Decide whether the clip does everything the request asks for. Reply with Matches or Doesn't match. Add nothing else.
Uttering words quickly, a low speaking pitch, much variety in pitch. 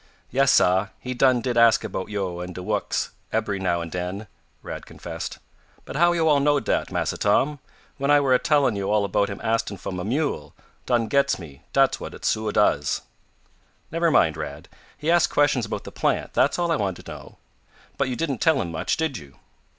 Matches